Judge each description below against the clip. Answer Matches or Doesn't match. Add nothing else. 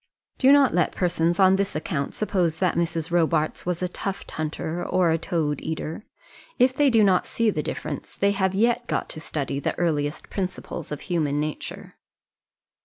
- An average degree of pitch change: Matches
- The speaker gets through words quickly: Doesn't match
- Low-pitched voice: Doesn't match